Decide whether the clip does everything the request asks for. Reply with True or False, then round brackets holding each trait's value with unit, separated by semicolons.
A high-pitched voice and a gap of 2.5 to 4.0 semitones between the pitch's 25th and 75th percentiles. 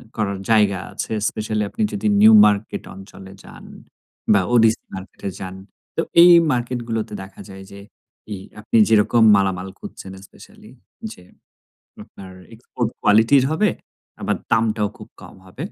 False (105 Hz; 2.9 semitones)